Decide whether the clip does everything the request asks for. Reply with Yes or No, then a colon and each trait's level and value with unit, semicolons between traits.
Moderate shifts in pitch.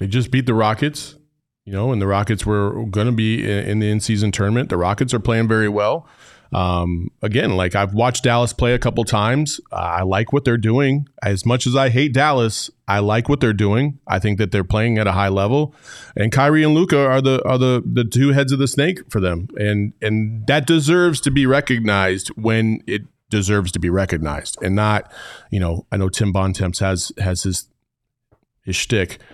Yes: average, 4.6 semitones